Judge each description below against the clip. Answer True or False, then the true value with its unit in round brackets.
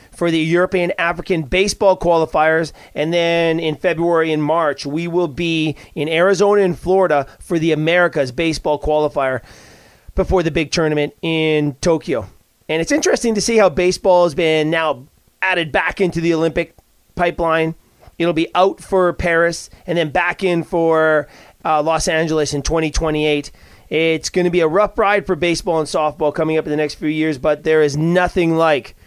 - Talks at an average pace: True (175 wpm)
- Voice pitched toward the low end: False (165 Hz)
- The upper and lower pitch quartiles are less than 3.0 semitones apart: True (2.4 semitones)